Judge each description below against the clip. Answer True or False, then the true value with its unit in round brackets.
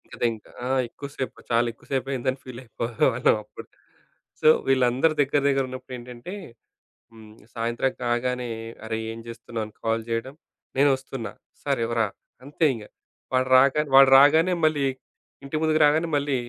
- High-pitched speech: False (130 Hz)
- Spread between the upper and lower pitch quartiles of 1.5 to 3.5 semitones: True (2.9 semitones)